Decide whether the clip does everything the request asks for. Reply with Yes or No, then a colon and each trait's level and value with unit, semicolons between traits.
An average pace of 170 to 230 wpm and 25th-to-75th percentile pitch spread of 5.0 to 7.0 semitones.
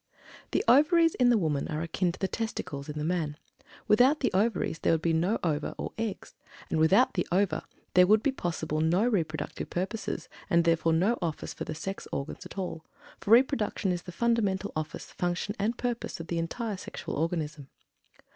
Yes: average, 190 wpm; wide, 5.5 semitones